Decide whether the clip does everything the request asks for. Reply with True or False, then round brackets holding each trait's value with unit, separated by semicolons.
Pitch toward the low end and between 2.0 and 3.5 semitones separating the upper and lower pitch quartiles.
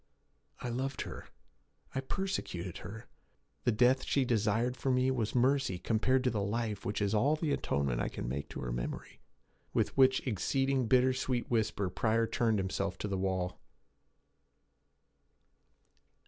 False (115 Hz; 4.9 semitones)